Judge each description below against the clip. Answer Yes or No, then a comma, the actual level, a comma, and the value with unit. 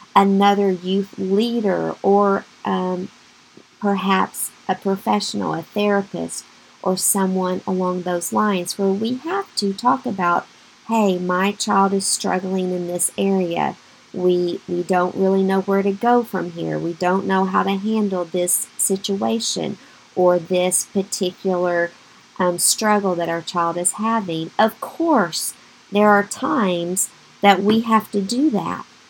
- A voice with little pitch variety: Yes, narrow, 2.2 semitones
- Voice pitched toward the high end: Yes, high, 195 Hz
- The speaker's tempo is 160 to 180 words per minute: No, average, 140 wpm